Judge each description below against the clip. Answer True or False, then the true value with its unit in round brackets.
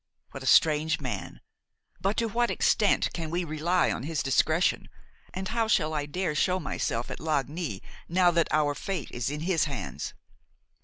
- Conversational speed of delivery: True (170 wpm)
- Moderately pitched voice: True (160 Hz)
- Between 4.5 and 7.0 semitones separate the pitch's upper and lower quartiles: False (3.9 semitones)